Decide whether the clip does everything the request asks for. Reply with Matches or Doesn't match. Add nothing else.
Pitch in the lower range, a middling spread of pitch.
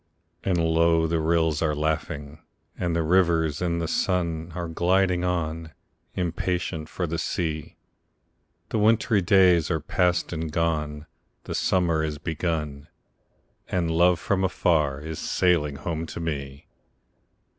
Doesn't match